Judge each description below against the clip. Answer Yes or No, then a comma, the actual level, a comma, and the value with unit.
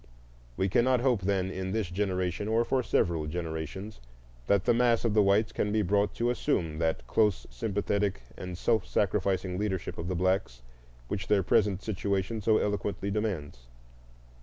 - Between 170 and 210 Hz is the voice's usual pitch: No, low, 100 Hz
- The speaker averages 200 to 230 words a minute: No, average, 160 wpm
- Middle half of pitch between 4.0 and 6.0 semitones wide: No, average, 2.8 semitones